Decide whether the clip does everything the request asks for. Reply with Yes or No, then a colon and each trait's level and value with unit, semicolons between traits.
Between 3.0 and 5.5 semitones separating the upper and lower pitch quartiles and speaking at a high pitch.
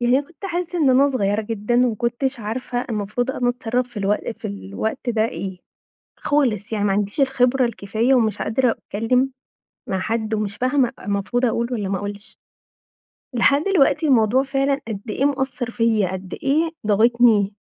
Yes: average, 4.2 semitones; high, 235 Hz